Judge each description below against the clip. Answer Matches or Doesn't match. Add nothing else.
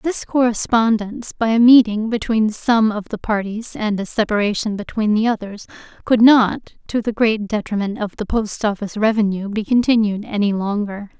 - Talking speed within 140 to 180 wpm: Matches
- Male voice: Doesn't match